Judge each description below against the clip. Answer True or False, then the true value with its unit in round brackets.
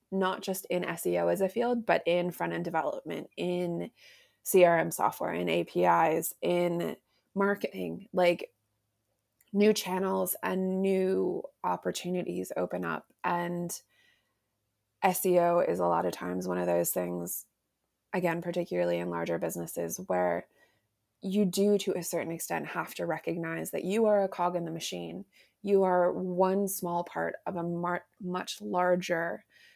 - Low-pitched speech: False (175 Hz)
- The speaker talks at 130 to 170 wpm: True (145 wpm)